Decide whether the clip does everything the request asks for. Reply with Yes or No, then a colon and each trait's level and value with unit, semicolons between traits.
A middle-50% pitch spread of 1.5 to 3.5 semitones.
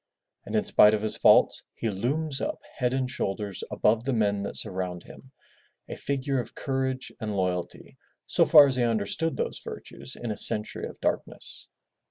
No: average, 4.6 semitones